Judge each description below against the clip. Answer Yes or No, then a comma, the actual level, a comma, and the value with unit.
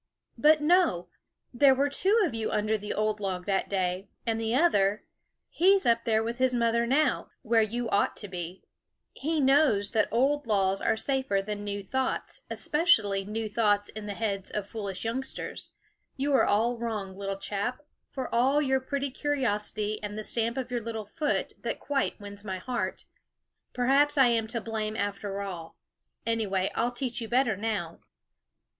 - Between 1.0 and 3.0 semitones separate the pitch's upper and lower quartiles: No, average, 4.4 semitones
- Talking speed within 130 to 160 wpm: No, average, 175 wpm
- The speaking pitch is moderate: No, high, 225 Hz